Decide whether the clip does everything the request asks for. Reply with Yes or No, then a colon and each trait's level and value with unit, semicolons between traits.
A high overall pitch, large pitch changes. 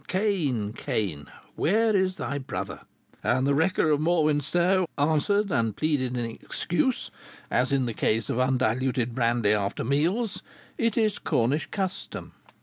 No: medium, 140 Hz; wide, 7.6 semitones